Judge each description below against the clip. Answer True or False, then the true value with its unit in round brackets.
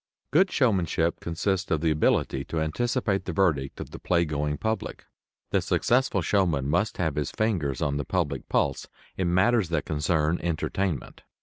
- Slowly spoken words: False (160 wpm)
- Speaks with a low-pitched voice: True (85 Hz)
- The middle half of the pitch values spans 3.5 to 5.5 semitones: True (4.6 semitones)